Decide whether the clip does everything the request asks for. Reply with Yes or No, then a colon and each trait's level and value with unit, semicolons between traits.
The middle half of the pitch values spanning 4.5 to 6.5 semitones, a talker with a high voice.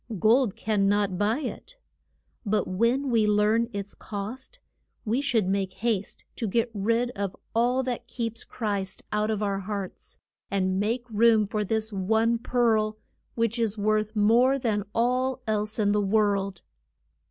No: narrow, 2.5 semitones; high, 215 Hz